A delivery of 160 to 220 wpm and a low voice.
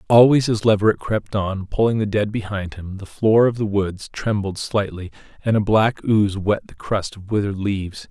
Yes: average, 200 wpm; low, 105 Hz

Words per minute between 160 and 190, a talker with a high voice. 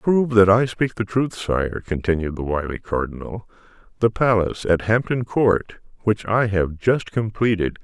No: average, 170 wpm; low, 105 Hz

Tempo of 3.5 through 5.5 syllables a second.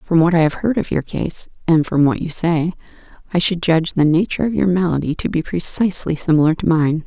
No: 6.0 syllables/s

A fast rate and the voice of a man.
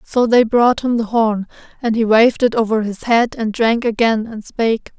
No: fast, 215 wpm; female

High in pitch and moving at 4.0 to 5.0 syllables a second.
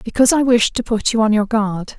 No: high, 225 Hz; 5.8 syllables/s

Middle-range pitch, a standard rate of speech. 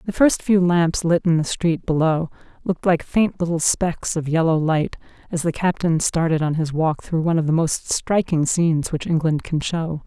No: medium, 165 Hz; fast, 210 wpm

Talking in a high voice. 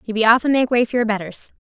Yes: high, 230 Hz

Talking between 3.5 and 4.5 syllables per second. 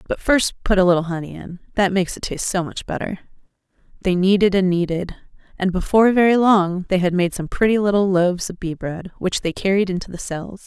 No: 5.9 syllables/s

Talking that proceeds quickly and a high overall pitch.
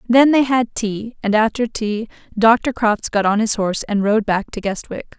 Yes: fast, 210 wpm; high, 220 Hz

